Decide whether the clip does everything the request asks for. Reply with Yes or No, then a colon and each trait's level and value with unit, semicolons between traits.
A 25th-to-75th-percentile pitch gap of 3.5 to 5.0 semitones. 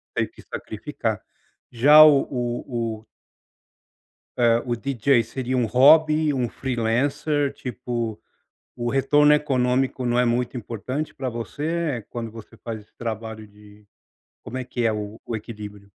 No: average, 3.1 semitones